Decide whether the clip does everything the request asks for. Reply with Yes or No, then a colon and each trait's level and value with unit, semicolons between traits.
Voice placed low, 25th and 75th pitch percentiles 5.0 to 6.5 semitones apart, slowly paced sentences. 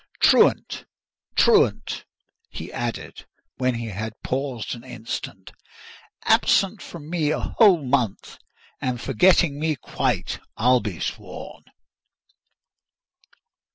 Yes: low, 130 Hz; wide, 5.6 semitones; slow, 100 wpm